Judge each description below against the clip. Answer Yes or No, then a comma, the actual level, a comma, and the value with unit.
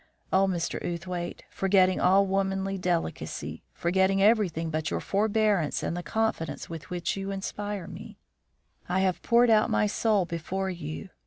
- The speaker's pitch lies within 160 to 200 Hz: Yes, high, 190 Hz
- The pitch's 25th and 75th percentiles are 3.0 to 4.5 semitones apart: No, narrow, 2.5 semitones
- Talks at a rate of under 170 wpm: Yes, average, 150 wpm